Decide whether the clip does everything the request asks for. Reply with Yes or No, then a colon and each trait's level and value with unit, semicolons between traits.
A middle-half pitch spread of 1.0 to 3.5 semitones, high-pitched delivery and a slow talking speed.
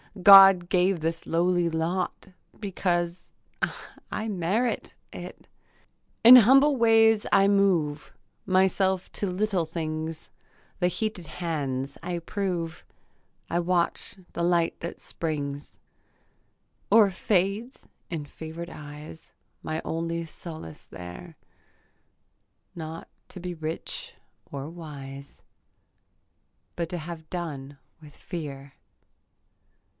No: average, 3.2 semitones; medium, 170 Hz; slow, 100 wpm